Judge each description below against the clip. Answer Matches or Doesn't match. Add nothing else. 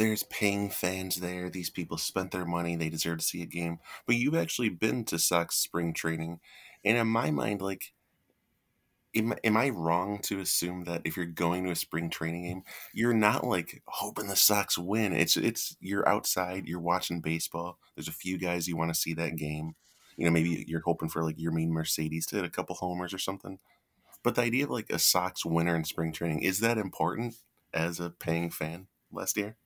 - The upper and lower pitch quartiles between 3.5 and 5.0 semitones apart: Doesn't match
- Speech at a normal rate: Doesn't match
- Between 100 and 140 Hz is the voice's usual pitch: Doesn't match